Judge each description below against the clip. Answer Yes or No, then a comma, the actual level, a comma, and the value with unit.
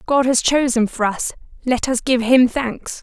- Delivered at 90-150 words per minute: No, average, 200 wpm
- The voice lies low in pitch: No, very high, 250 Hz